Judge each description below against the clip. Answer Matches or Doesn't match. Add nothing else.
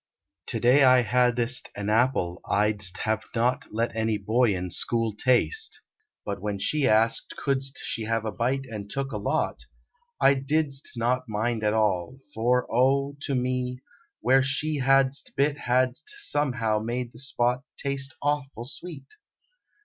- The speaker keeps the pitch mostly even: Doesn't match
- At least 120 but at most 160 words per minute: Matches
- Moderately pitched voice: Doesn't match